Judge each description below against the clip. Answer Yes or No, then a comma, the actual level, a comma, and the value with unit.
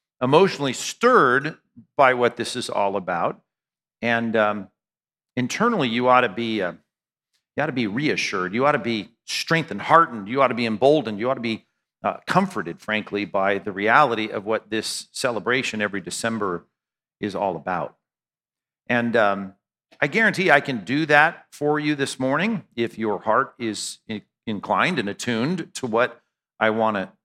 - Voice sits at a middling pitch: No, low, 115 Hz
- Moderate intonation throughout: Yes, average, 4.2 semitones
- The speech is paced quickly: No, average, 165 wpm